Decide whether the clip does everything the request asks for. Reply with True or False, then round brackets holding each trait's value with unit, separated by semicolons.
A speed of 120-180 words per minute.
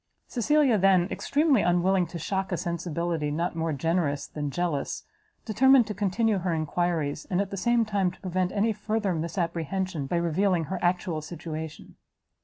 True (160 wpm)